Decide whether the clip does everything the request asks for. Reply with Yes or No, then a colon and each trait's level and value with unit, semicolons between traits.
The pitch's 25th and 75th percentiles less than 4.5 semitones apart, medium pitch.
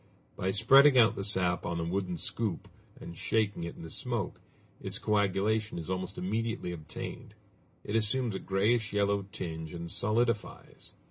No: average, 3.9 semitones; low, 100 Hz